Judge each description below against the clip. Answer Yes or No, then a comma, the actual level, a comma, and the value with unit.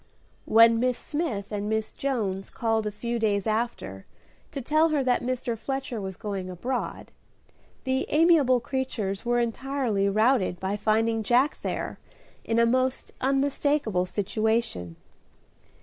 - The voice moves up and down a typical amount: Yes, average, 4.1 semitones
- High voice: Yes, high, 230 Hz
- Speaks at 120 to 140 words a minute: Yes, slow, 135 wpm